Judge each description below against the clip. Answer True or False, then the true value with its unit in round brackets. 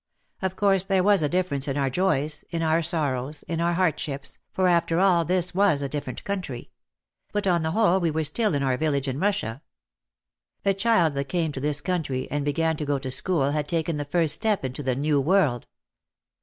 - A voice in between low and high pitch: True (160 Hz)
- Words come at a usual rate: False (210 wpm)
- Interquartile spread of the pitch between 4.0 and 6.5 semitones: True (4.5 semitones)